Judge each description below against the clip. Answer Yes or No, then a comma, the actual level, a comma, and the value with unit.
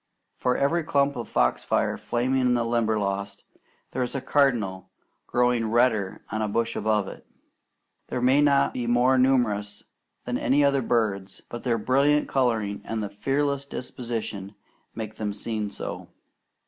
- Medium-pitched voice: No, low, 120 Hz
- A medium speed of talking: Yes, average, 145 wpm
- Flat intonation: No, average, 3.8 semitones